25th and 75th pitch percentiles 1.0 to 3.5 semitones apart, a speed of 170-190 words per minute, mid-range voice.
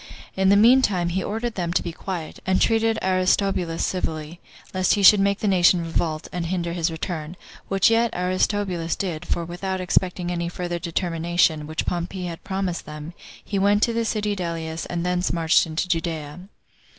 Yes: narrow, 2.5 semitones; average, 180 wpm; medium, 180 Hz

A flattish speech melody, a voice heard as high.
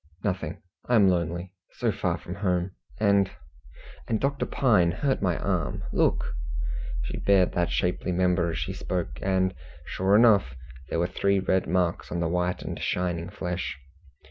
No: narrow, 2.2 semitones; very low, 90 Hz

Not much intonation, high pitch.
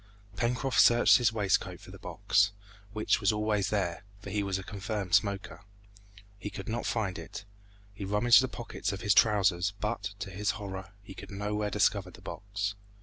No: narrow, 1.6 semitones; low, 100 Hz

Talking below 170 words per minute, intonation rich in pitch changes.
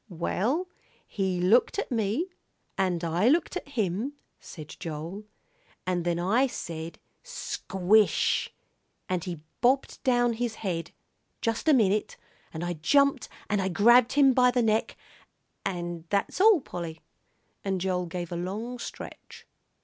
Yes: average, 140 wpm; wide, 5.8 semitones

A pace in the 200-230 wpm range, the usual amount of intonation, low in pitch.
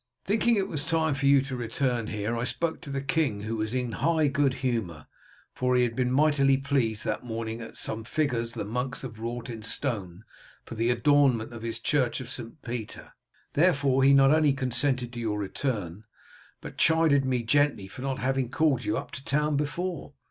Yes: fast, 205 wpm; average, 3.8 semitones; low, 130 Hz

